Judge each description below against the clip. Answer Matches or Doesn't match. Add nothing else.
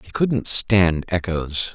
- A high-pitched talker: Doesn't match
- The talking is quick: Doesn't match